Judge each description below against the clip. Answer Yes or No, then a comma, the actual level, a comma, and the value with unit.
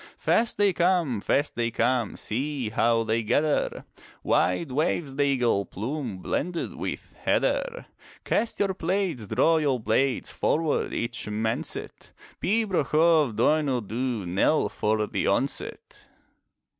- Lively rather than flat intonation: Yes, wide, 6.4 semitones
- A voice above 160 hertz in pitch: No, low, 135 Hz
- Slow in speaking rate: Yes, slow, 130 wpm